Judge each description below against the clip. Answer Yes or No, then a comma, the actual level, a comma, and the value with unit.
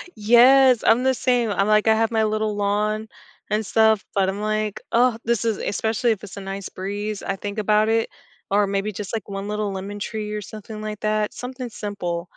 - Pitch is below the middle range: No, high, 215 Hz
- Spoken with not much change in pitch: Yes, narrow, 1.6 semitones